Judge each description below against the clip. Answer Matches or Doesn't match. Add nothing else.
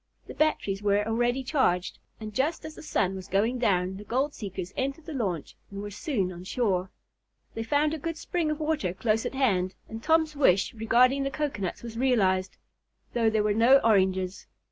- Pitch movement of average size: Doesn't match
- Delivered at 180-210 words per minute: Matches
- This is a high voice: Matches